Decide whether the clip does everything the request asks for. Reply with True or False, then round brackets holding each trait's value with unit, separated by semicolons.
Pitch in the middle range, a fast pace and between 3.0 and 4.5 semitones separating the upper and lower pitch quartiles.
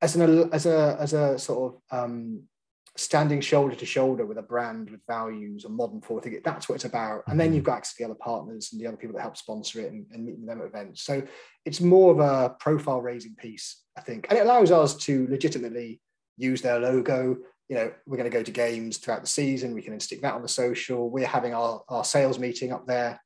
False (130 Hz; 240 wpm; 3.9 semitones)